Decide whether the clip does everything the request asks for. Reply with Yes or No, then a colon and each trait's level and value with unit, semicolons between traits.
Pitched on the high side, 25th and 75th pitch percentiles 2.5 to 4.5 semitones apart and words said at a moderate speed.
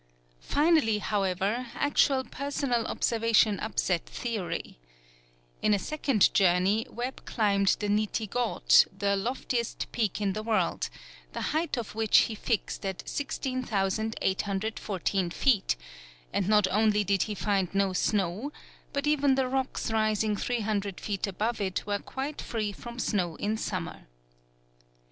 No: high, 215 Hz; average, 3.4 semitones; slow, 130 wpm